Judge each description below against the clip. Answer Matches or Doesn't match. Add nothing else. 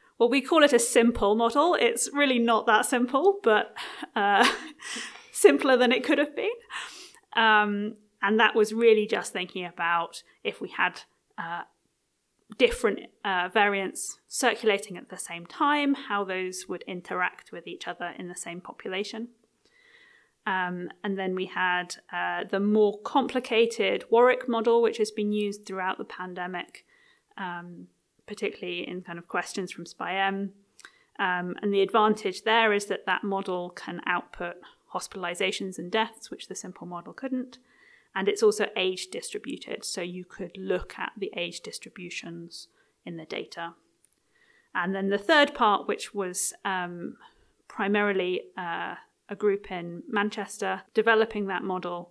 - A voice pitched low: Doesn't match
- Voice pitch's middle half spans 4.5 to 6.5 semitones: Matches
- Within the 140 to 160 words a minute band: Matches